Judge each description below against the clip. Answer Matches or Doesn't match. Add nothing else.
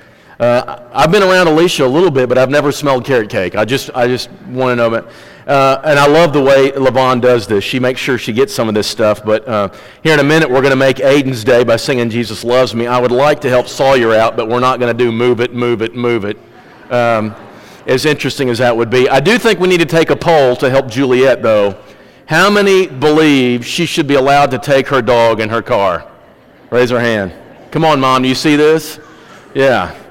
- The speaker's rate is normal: Doesn't match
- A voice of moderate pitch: Doesn't match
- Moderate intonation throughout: Matches